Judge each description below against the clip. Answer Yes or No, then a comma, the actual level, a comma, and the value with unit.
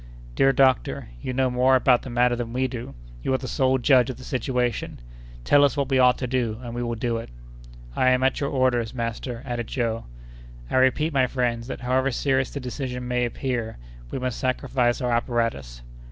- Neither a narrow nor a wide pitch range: No, narrow, 1.6 semitones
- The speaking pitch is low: Yes, low, 125 Hz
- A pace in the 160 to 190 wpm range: No, fast, 205 wpm